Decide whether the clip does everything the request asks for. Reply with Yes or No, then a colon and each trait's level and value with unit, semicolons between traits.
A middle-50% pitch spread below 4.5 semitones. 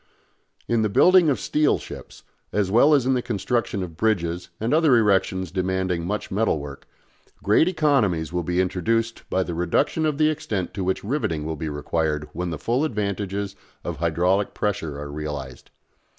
No: wide, 5.5 semitones